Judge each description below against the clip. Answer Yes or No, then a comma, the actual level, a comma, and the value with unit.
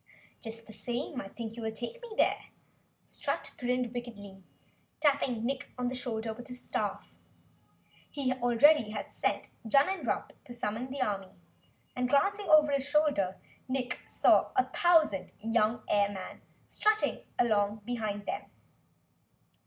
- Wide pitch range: No, average, 4.1 semitones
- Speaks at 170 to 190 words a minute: No, slow, 135 wpm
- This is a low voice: No, high, 245 Hz